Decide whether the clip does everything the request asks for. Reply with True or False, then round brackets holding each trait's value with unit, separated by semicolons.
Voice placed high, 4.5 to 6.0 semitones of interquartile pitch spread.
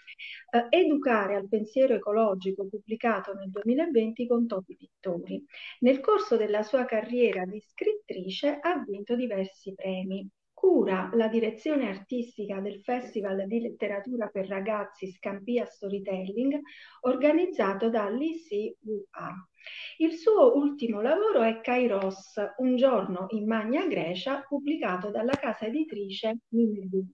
True (225 Hz; 4.9 semitones)